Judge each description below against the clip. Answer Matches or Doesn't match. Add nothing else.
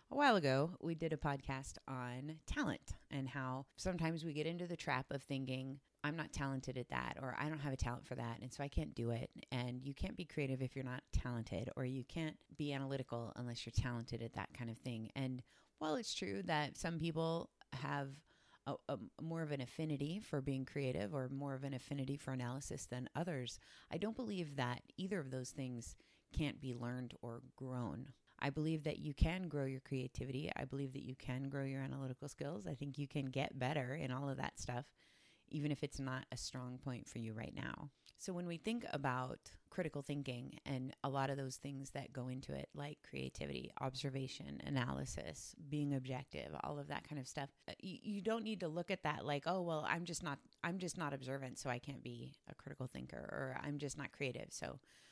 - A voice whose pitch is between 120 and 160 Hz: Matches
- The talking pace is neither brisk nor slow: Doesn't match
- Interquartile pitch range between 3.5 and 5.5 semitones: Doesn't match